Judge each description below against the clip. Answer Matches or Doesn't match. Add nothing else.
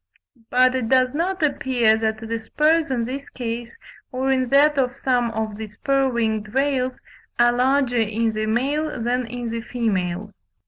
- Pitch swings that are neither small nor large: Matches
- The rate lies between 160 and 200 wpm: Matches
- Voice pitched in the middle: Doesn't match